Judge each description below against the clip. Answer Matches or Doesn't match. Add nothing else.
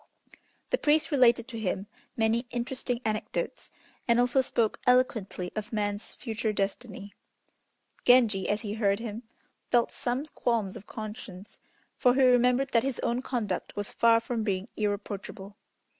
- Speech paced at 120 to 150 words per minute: Matches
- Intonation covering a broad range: Doesn't match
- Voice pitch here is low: Doesn't match